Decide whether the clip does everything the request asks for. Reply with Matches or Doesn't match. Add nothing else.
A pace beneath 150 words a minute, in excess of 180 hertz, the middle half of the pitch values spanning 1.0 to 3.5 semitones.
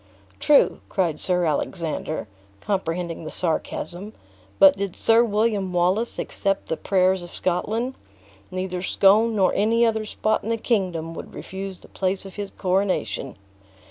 Matches